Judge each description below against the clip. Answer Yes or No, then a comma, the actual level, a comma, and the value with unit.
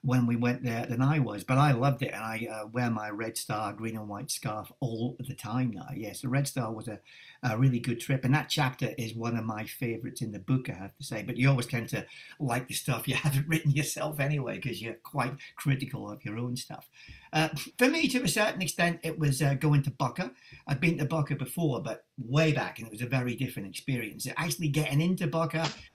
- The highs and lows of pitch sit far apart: No, average, 4.0 semitones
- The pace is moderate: No, fast, 240 wpm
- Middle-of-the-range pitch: No, low, 130 Hz